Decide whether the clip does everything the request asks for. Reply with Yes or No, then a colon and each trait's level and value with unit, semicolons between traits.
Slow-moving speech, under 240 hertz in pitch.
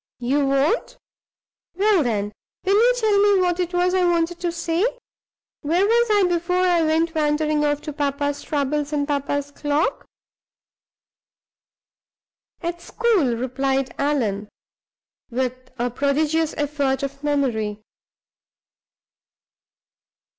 No: slow, 115 wpm; very high, 295 Hz